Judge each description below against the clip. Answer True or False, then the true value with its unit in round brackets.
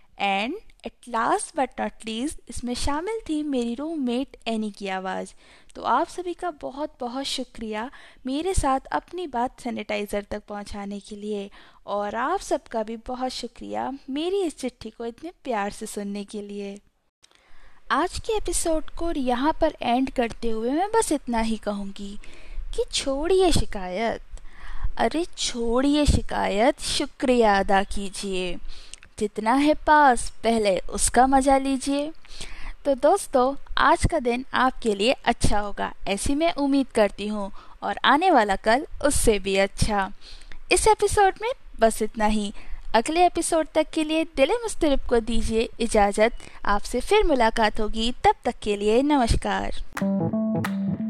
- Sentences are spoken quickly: False (145 wpm)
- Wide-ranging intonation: True (6.3 semitones)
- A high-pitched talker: True (245 Hz)